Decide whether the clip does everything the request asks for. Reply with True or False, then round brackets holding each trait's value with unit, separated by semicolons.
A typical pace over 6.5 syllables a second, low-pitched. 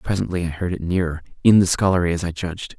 True (6.8 syllables/s; 90 Hz)